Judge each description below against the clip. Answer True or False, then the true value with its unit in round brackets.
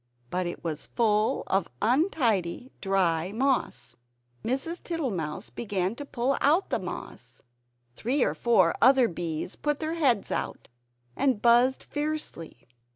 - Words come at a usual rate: False (130 wpm)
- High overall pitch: True (235 Hz)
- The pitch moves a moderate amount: False (6.9 semitones)